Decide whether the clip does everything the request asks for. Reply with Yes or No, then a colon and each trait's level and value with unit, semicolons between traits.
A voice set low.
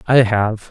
Yes: low, 110 Hz